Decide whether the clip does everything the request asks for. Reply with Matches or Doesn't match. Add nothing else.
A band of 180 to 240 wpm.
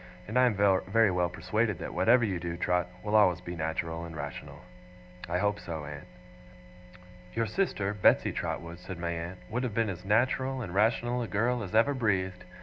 Matches